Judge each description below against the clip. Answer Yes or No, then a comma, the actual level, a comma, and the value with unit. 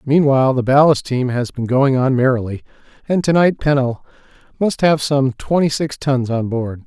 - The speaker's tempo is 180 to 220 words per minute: Yes, average, 185 wpm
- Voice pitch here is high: No, low, 135 Hz